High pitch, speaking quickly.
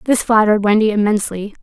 No: high, 215 Hz; average, 150 wpm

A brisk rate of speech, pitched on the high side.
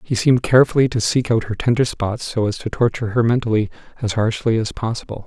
No: fast, 215 wpm; low, 115 Hz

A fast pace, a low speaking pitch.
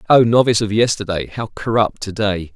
No: average, 190 wpm; low, 105 Hz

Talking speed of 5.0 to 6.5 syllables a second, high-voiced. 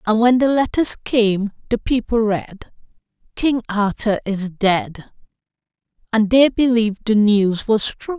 No: 3.9 syllables/s; high, 220 Hz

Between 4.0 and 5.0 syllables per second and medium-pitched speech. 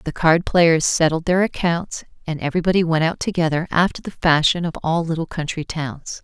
No: 5.4 syllables/s; medium, 165 Hz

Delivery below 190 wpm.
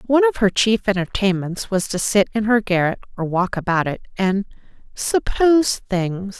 Yes: average, 170 wpm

